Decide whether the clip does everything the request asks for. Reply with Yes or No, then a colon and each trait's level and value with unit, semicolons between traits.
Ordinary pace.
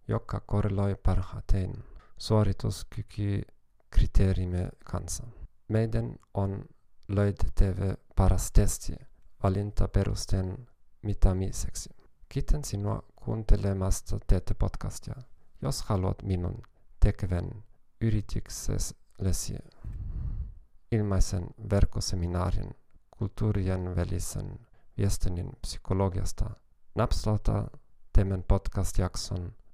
No: slow, 65 wpm